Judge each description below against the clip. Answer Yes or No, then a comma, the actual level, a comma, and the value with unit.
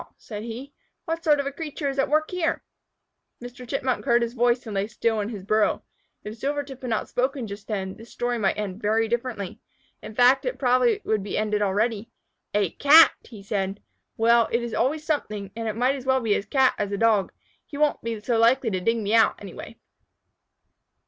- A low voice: No, high, 230 Hz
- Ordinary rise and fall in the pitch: Yes, average, 3.9 semitones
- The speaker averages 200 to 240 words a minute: Yes, fast, 205 wpm